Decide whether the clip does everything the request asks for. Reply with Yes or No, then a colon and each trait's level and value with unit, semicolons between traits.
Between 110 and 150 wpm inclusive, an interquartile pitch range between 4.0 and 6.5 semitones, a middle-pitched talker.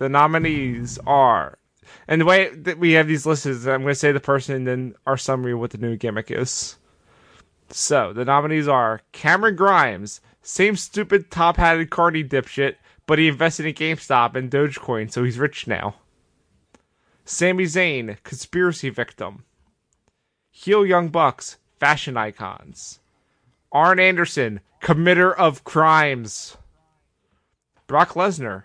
Yes: average, 140 wpm; average, 5.2 semitones; medium, 145 Hz